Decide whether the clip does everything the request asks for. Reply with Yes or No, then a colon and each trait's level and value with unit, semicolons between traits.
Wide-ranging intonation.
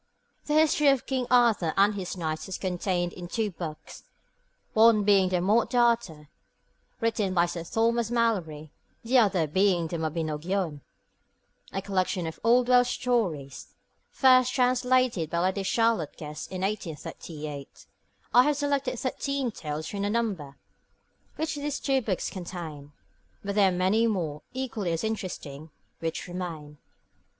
Yes: wide, 6.1 semitones